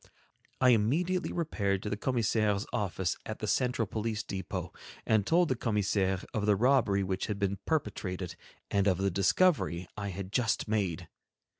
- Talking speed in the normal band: Yes, average, 160 wpm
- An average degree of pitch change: Yes, average, 3.6 semitones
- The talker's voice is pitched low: Yes, low, 105 Hz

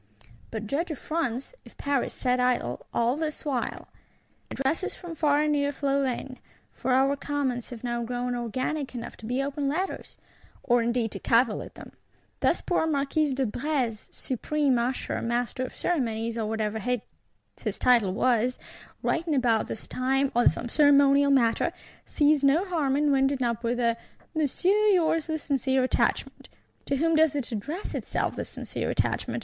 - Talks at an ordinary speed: Yes, average, 160 wpm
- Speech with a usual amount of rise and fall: Yes, average, 3.5 semitones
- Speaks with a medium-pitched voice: No, very high, 265 Hz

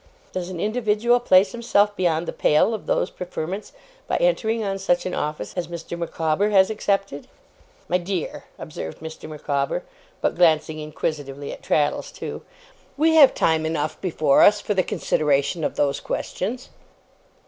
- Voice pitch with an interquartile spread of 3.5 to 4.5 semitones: No, average, 5.1 semitones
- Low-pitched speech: No, medium, 175 Hz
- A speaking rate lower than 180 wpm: Yes, average, 155 wpm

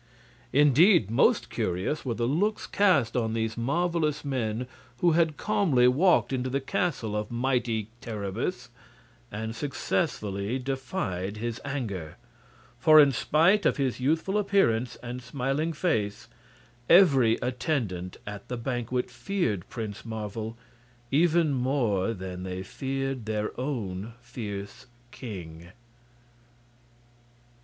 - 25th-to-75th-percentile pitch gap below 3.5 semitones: No, wide, 5.4 semitones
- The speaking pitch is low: Yes, low, 125 Hz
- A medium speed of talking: No, slow, 115 wpm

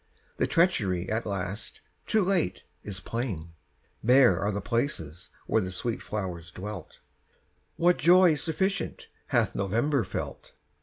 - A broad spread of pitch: Yes, wide, 8.4 semitones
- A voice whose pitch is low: Yes, low, 110 Hz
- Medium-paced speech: No, slow, 125 wpm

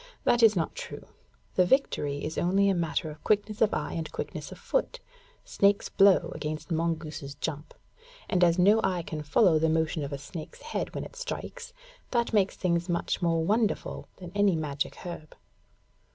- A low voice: No, medium, 175 Hz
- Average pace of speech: Yes, average, 180 wpm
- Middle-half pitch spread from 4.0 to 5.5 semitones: Yes, average, 4.4 semitones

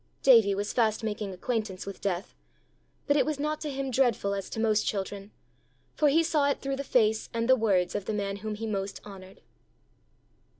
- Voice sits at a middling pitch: No, high, 215 Hz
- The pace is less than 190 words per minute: No, average, 195 wpm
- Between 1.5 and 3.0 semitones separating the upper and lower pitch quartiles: No, average, 4.9 semitones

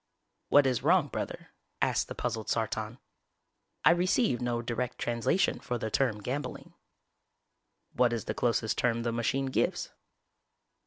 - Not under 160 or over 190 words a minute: No, average, 140 wpm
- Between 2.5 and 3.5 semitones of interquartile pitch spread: Yes, average, 2.8 semitones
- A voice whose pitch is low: Yes, low, 120 Hz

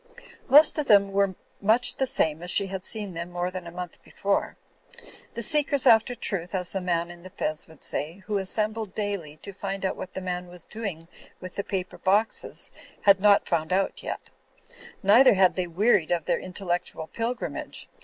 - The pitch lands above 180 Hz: Yes, high, 190 Hz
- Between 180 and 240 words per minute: Yes, average, 190 wpm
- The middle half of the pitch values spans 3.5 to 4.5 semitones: No, average, 2.9 semitones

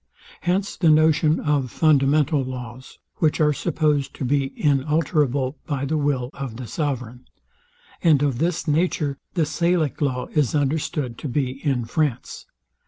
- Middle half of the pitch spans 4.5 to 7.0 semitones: No, average, 3.0 semitones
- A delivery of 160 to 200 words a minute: No, average, 145 wpm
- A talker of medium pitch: Yes, medium, 145 Hz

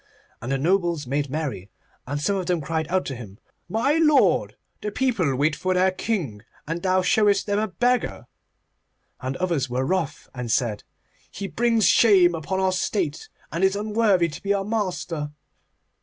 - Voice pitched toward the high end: No, medium, 180 Hz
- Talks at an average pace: Yes, average, 170 wpm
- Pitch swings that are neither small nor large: No, wide, 5.7 semitones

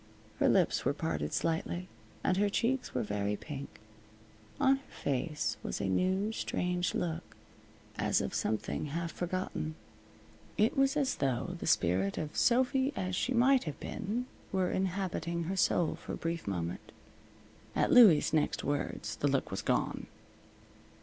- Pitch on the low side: No, medium, 175 Hz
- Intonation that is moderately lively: No, wide, 6.3 semitones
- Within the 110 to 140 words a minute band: No, average, 150 wpm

